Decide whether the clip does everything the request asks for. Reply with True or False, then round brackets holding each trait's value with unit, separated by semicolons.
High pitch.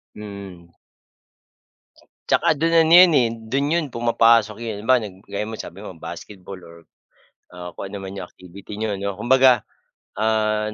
False (105 Hz)